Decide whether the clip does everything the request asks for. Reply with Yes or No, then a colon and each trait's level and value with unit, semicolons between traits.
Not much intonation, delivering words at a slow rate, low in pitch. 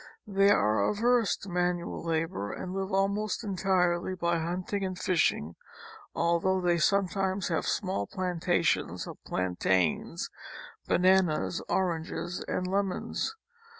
No: narrow, 2.3 semitones; slow, 115 wpm; medium, 180 Hz